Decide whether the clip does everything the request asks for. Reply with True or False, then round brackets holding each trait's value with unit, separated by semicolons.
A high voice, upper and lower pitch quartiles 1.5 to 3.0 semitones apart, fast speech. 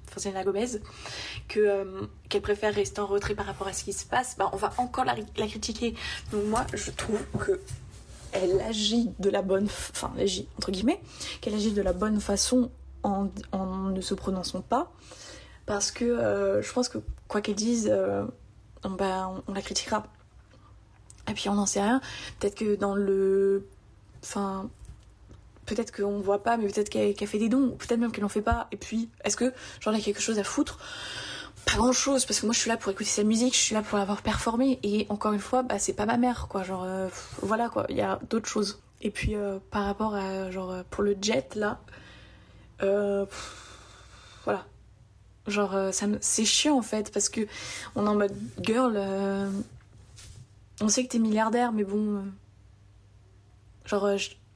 False (205 Hz; 2.6 semitones; 205 wpm)